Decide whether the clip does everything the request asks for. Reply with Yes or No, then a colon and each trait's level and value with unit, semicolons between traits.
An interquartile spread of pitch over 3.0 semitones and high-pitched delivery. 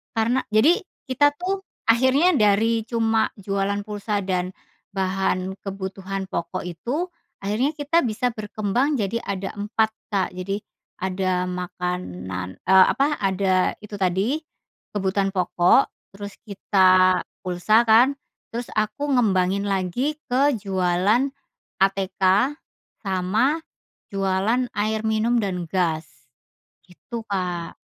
Yes: average, 3.7 semitones; high, 200 Hz